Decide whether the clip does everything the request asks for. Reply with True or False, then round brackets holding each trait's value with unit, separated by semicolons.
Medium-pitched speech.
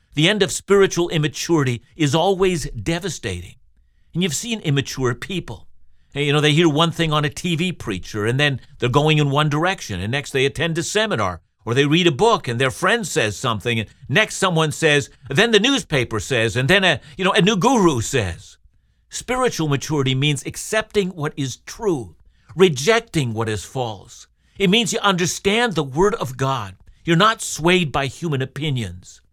True (150 Hz)